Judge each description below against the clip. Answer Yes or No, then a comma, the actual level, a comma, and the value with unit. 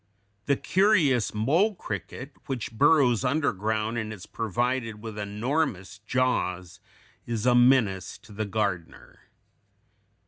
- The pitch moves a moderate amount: Yes, average, 4.0 semitones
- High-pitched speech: No, low, 115 Hz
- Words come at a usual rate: No, slow, 110 wpm